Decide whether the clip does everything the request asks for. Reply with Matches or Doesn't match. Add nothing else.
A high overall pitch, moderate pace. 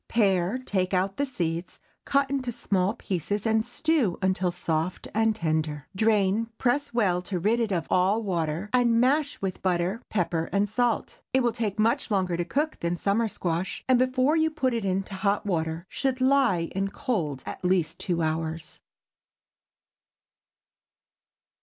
Matches